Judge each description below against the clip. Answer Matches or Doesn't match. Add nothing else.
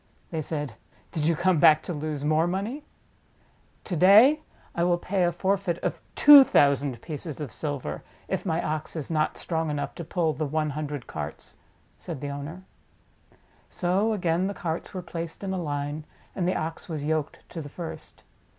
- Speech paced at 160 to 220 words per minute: Matches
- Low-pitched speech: Doesn't match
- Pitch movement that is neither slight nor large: Matches